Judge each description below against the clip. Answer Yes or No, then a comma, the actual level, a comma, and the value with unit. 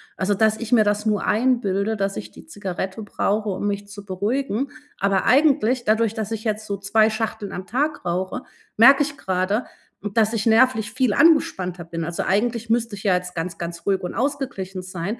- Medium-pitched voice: No, high, 210 Hz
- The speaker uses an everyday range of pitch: Yes, average, 3.5 semitones